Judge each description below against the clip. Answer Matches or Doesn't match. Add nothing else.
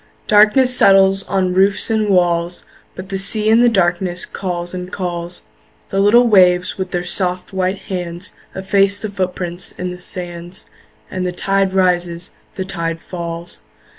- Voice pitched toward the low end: Doesn't match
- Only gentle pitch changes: Matches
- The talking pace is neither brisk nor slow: Matches